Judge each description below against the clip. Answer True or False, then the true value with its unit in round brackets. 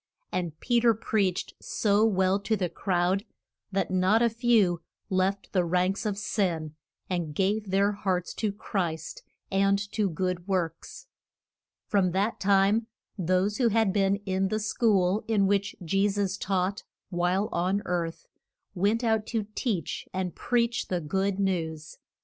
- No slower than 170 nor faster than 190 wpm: False (150 wpm)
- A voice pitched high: True (195 Hz)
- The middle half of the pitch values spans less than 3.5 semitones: True (2.5 semitones)